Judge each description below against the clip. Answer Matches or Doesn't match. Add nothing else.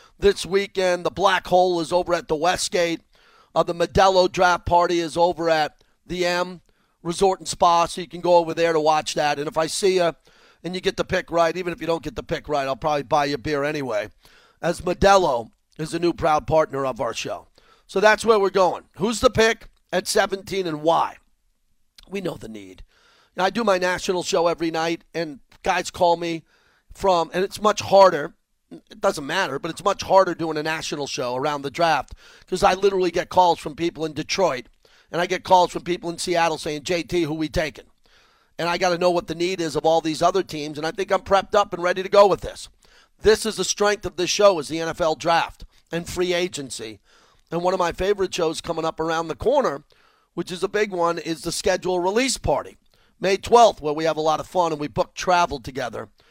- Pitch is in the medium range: Matches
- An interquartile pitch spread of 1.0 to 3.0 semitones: Matches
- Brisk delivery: Matches